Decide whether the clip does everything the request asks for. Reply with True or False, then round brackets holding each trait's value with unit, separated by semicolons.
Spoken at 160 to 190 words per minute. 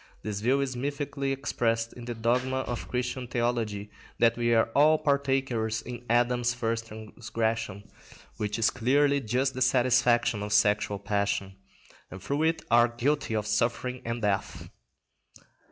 False (145 wpm)